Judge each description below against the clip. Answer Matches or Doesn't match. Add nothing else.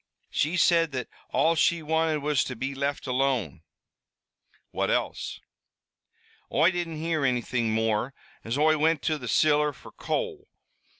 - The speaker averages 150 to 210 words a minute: Doesn't match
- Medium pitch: Matches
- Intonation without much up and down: Doesn't match